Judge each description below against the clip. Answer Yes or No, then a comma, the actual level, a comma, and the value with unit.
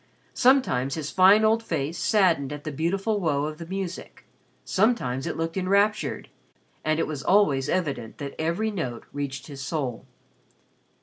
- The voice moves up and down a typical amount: No, wide, 5.8 semitones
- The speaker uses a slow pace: No, average, 150 wpm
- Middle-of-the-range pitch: Yes, medium, 165 Hz